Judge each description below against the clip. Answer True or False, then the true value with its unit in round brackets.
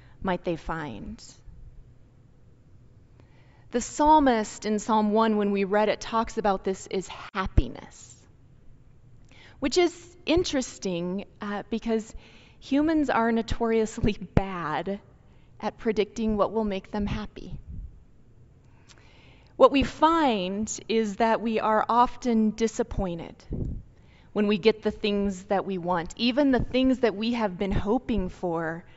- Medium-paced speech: False (120 wpm)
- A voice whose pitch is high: True (210 Hz)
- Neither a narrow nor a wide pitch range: True (4.0 semitones)